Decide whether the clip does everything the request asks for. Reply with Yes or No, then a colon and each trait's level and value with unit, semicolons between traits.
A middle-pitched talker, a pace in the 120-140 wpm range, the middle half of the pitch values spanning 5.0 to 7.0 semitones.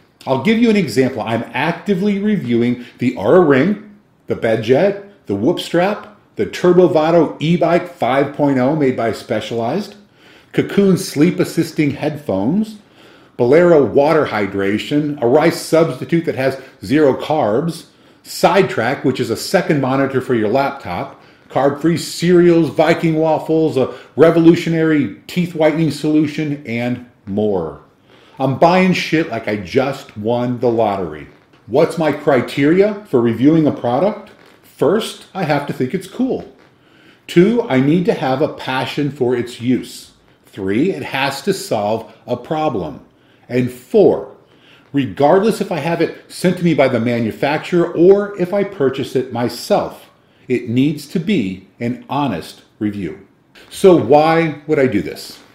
Yes: medium, 150 Hz; slow, 135 wpm; average, 5.3 semitones